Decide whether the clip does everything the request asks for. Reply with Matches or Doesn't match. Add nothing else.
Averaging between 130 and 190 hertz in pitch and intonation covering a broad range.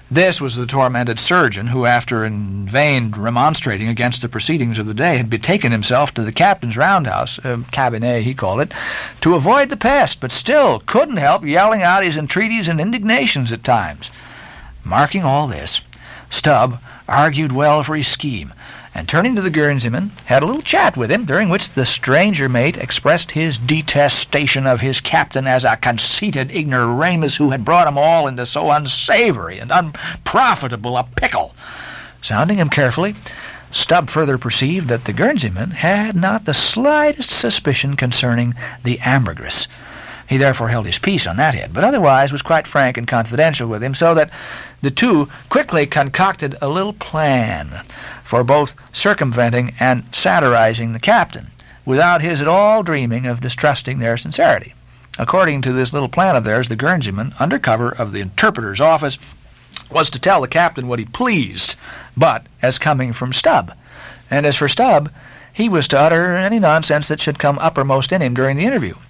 Doesn't match